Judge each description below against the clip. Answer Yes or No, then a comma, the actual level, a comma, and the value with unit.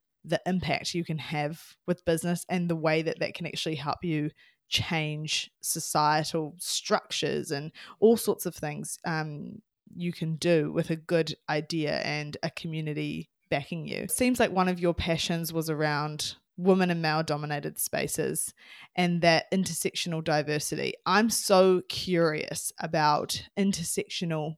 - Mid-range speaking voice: Yes, medium, 165 Hz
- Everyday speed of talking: Yes, average, 145 wpm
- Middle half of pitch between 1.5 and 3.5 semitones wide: Yes, average, 2.8 semitones